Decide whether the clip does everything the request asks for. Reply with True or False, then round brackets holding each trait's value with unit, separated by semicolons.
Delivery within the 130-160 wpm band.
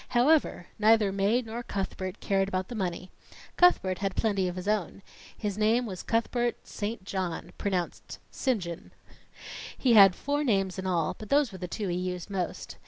False (175 wpm)